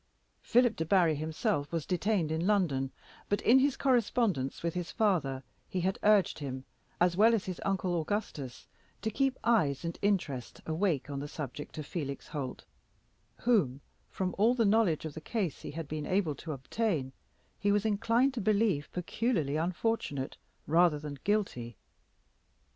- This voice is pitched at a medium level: Yes, medium, 175 Hz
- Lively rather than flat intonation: Yes, wide, 6.4 semitones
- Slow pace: No, average, 160 wpm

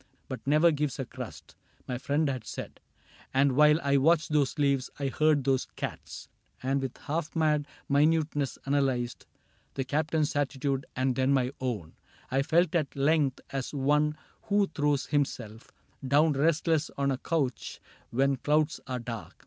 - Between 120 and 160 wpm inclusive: Yes, average, 155 wpm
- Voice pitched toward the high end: No, medium, 140 Hz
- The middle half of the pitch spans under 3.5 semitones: Yes, narrow, 2.4 semitones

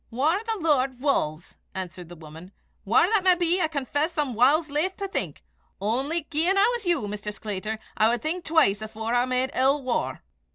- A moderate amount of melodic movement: No, wide, 7.3 semitones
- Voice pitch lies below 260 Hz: No, very high, 265 Hz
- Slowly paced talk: No, average, 195 wpm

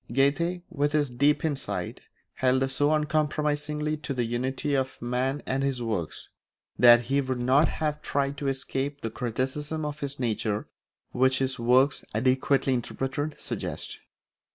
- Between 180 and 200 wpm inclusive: No, average, 145 wpm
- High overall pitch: No, low, 135 Hz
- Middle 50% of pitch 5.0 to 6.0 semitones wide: No, narrow, 2.5 semitones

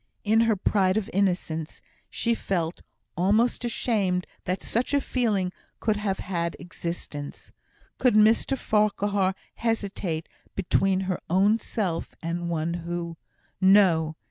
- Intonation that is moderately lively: Yes, average, 3.6 semitones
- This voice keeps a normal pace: No, slow, 120 wpm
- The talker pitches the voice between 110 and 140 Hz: No, high, 190 Hz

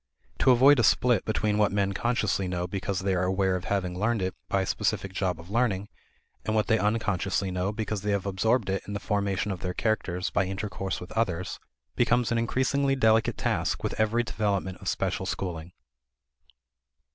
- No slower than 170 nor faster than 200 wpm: Yes, average, 190 wpm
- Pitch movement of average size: Yes, average, 3.0 semitones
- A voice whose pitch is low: Yes, low, 100 Hz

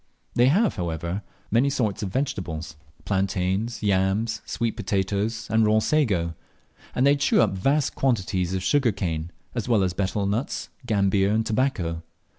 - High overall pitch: No, low, 105 Hz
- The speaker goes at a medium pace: Yes, average, 150 wpm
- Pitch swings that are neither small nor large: Yes, average, 4.0 semitones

